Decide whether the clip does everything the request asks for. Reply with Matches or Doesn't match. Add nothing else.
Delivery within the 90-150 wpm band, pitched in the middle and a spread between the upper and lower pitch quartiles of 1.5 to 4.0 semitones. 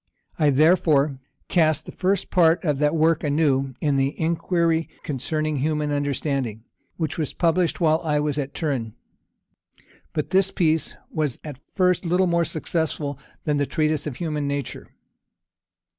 Matches